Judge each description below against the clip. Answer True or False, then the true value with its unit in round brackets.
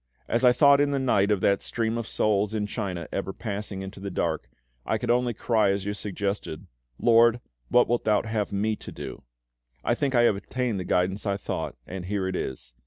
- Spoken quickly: True (220 wpm)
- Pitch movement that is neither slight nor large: True (3.2 semitones)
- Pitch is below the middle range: True (105 Hz)